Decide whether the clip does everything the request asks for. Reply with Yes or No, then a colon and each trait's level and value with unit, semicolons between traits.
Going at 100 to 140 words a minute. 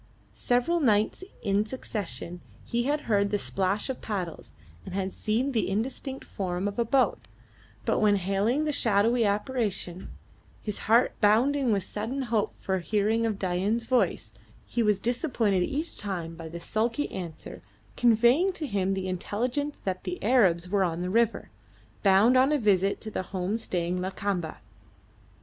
No: average, 155 wpm